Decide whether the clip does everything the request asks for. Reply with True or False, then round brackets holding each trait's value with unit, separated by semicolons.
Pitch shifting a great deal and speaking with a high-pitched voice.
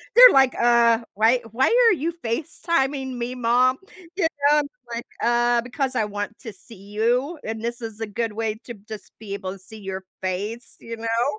False (2.9 semitones; 235 Hz)